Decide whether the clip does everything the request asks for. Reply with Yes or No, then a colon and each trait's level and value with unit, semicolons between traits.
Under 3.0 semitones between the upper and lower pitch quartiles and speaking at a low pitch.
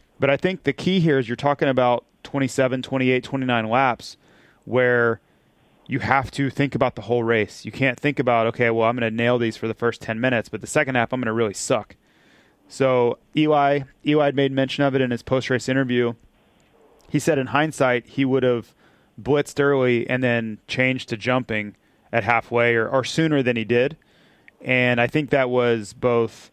Yes: narrow, 2.6 semitones; low, 125 Hz